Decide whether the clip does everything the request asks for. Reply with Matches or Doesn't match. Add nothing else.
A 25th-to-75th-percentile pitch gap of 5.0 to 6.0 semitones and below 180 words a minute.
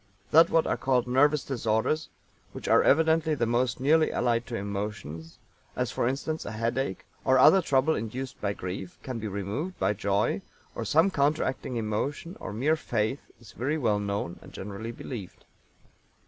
Matches